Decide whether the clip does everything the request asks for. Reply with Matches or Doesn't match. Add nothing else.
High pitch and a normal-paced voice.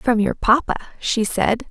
Matches